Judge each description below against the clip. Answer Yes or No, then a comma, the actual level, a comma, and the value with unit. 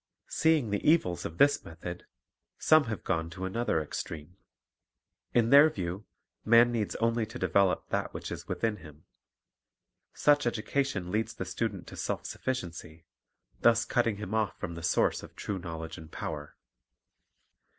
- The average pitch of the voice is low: Yes, low, 105 Hz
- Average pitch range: No, wide, 5.9 semitones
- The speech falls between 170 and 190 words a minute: No, average, 150 wpm